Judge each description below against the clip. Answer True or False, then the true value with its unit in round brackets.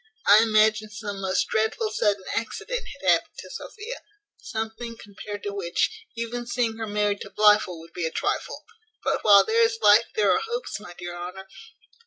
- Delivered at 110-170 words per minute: False (180 wpm)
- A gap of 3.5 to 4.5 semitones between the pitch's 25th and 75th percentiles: False (2.5 semitones)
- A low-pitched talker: False (215 Hz)